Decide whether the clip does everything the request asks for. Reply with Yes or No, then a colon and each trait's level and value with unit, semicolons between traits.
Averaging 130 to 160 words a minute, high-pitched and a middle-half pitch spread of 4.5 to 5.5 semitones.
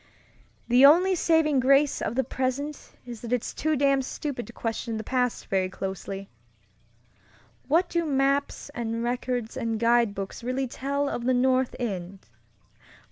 No: average, 145 wpm; very high, 250 Hz; average, 3.3 semitones